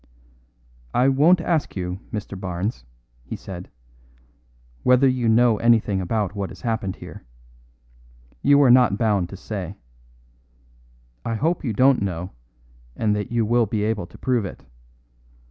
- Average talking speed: Yes, average, 145 wpm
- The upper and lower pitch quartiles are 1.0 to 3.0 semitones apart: No, average, 4.2 semitones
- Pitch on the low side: Yes, low, 110 Hz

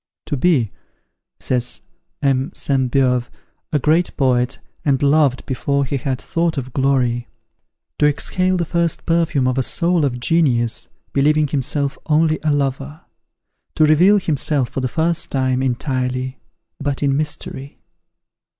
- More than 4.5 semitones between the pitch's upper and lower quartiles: No, average, 3.1 semitones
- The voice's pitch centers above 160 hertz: No, medium, 140 Hz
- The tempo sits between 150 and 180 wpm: No, average, 140 wpm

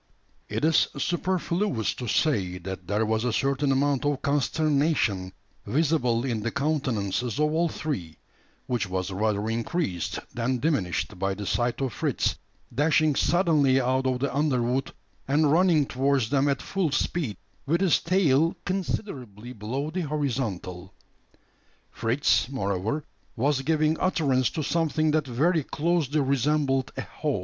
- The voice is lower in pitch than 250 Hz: Yes, low, 135 Hz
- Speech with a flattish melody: No, wide, 5.4 semitones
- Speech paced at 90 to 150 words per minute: Yes, average, 140 wpm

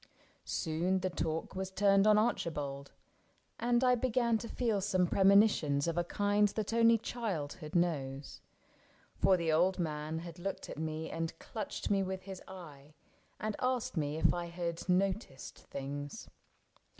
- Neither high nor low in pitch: Yes, medium, 180 Hz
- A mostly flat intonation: No, average, 4.5 semitones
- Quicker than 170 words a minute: No, average, 150 wpm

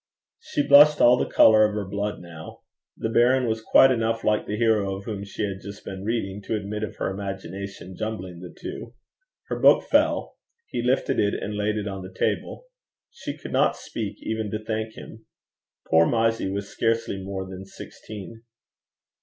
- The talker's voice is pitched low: Yes, low, 105 Hz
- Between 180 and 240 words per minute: Yes, average, 185 wpm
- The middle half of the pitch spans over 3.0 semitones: No, narrow, 2.5 semitones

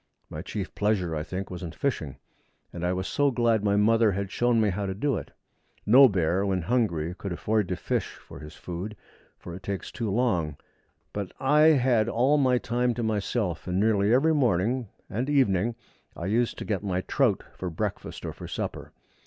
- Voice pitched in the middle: No, low, 105 Hz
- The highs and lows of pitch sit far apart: No, average, 4.7 semitones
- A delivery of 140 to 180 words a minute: No, average, 195 wpm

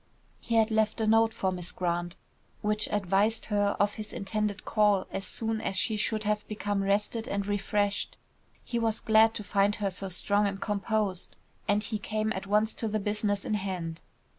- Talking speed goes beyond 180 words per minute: Yes, average, 190 wpm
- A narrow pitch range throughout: Yes, narrow, 1.6 semitones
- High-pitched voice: Yes, high, 210 Hz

